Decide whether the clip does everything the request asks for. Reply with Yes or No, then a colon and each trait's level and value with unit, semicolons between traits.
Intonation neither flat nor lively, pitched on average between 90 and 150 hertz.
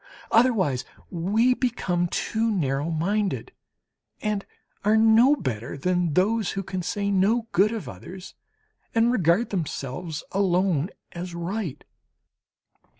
No: average, 4.4 semitones; high, 190 Hz